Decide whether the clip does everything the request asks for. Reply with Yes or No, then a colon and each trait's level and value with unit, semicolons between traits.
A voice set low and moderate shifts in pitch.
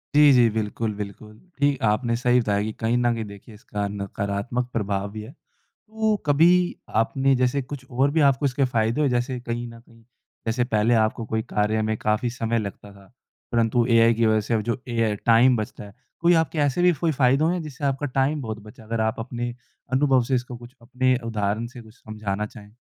Yes: low, 115 Hz; average, 3.2 semitones